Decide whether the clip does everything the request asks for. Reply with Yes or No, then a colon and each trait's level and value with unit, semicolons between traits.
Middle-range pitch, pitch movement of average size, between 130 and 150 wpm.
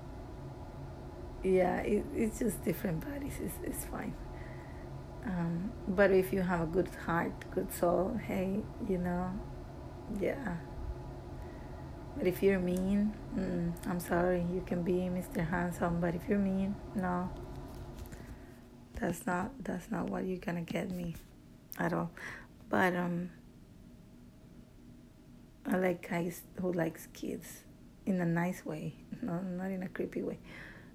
No: medium, 180 Hz; narrow, 1.6 semitones; slow, 135 wpm